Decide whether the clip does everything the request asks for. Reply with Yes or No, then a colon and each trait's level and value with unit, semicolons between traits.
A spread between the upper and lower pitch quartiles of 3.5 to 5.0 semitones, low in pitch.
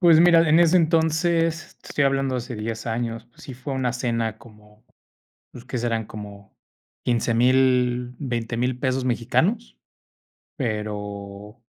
Yes: average, 3.8 semitones; low, 125 Hz